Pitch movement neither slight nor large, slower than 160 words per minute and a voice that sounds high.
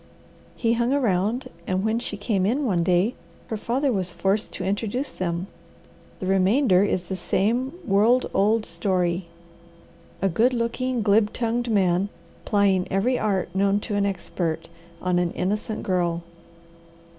Yes: average, 4.0 semitones; average, 145 wpm; high, 200 Hz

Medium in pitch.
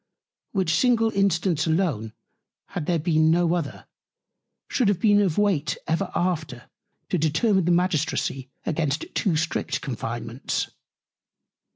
Yes: medium, 165 Hz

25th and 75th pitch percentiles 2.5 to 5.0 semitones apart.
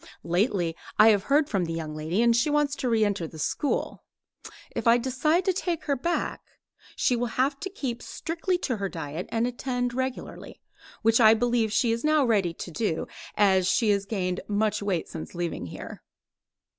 No: wide, 5.6 semitones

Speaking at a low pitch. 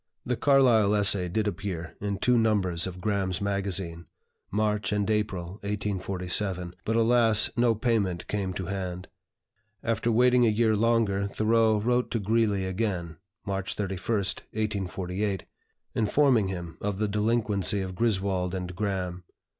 Yes: low, 100 Hz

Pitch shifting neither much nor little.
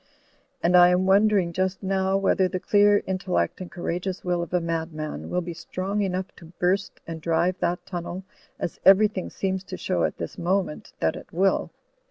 No: narrow, 1.9 semitones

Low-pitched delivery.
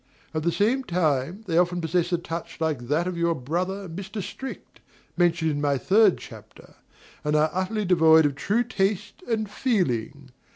No: medium, 175 Hz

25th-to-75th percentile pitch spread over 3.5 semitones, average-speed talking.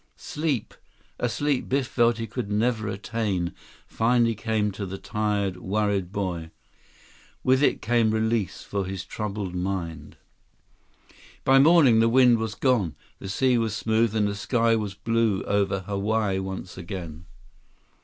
No: average, 3.2 semitones; average, 145 wpm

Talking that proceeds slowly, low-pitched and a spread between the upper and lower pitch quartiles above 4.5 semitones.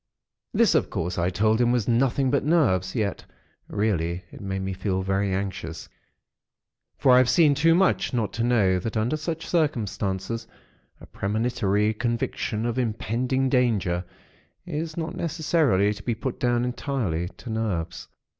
No: average, 155 wpm; low, 115 Hz; average, 5.2 semitones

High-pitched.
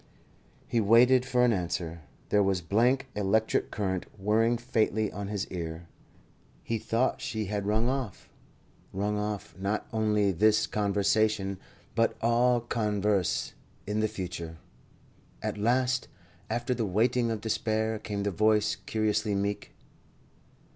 No: low, 105 Hz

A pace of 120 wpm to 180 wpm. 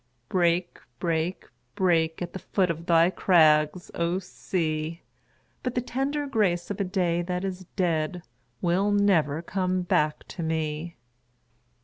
Yes: slow, 135 wpm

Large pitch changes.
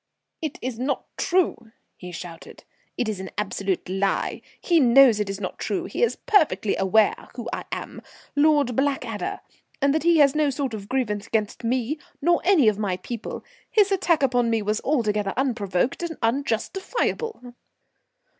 Yes: wide, 6.1 semitones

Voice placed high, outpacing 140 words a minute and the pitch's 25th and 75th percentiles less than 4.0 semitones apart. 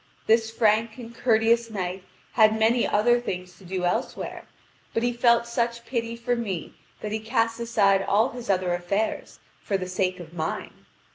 Yes: high, 220 Hz; average, 170 wpm; average, 3.6 semitones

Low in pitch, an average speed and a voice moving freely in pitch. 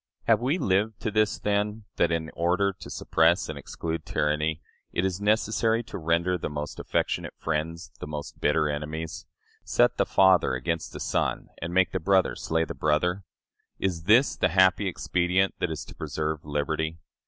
No: very low, 85 Hz; average, 175 wpm; average, 3.7 semitones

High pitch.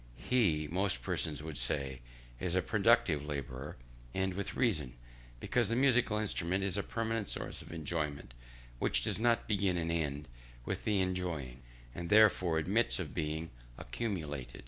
No: very low, 85 Hz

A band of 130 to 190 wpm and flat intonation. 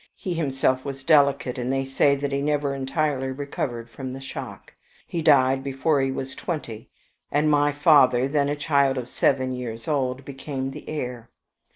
Yes: average, 175 wpm; narrow, 1.9 semitones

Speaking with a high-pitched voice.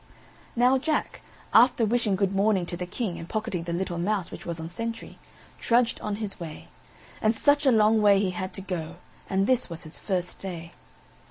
Yes: high, 195 Hz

